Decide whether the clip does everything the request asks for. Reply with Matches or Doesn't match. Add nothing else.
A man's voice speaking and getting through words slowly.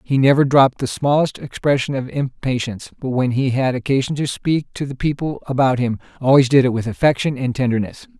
Doesn't match